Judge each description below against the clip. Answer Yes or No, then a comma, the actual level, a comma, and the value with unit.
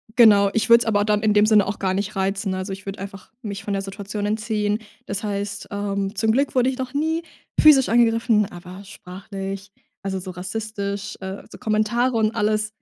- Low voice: No, high, 205 Hz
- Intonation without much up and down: Yes, narrow, 2.1 semitones